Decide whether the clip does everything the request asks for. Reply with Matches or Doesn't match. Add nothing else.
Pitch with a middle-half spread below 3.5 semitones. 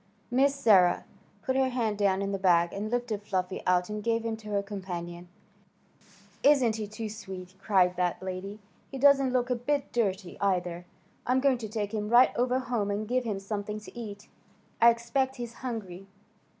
Doesn't match